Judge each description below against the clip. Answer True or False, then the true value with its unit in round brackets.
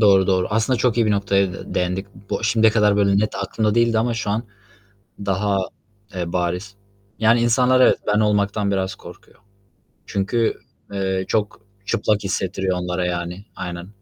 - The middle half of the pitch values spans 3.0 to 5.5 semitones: False (2.6 semitones)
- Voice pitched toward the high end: False (100 Hz)